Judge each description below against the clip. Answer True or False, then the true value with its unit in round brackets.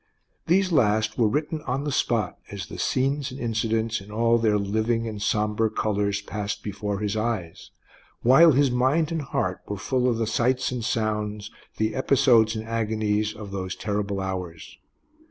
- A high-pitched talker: False (110 Hz)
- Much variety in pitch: False (3.2 semitones)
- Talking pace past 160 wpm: True (170 wpm)